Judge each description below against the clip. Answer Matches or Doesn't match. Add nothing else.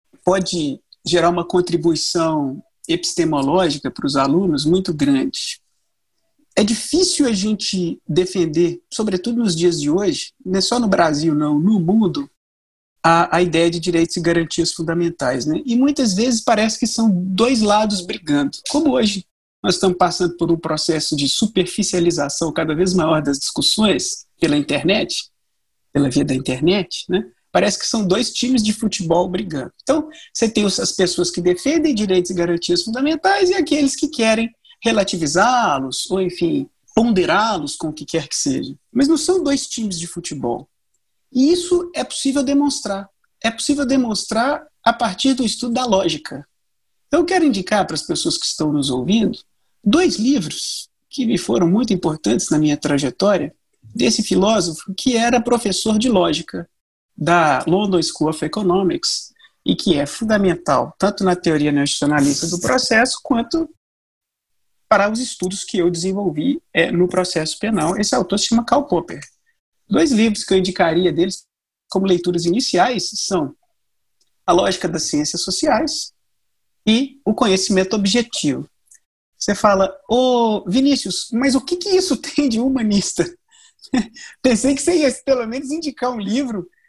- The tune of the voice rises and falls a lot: Matches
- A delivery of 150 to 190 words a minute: Matches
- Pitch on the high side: Matches